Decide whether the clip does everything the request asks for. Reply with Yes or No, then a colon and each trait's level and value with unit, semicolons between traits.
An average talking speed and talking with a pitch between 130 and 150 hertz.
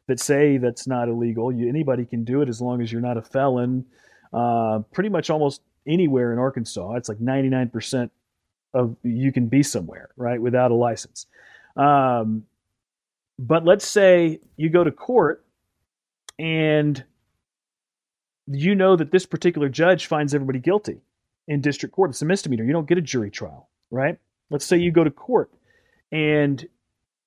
Yes: average, 165 wpm; low, 135 Hz